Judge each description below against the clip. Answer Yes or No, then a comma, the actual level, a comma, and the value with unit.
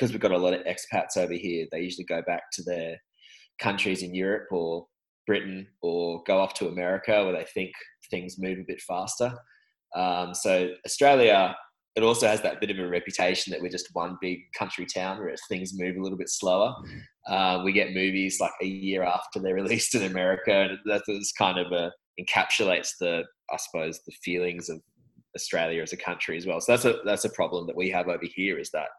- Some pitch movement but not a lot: No, narrow, 1.5 semitones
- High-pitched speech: No, very low, 95 Hz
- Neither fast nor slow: No, fast, 210 wpm